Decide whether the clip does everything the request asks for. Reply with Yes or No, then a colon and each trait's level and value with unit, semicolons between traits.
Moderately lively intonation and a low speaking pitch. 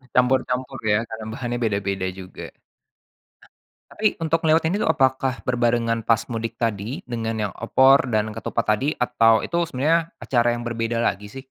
Yes: average, 3.0 semitones; low, 120 Hz